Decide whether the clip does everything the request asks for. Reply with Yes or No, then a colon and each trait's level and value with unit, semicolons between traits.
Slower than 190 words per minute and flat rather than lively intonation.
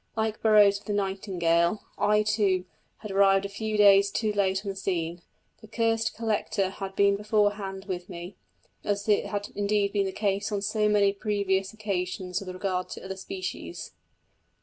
Yes: average, 170 wpm; narrow, 1.6 semitones